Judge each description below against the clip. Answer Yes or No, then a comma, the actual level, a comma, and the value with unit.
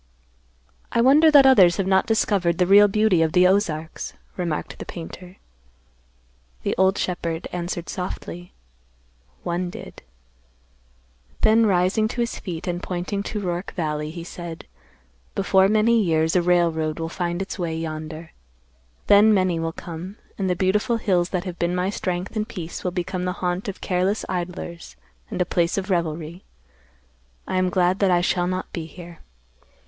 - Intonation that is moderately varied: No, narrow, 2.3 semitones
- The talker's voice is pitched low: No, medium, 180 Hz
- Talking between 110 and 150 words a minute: No, average, 165 wpm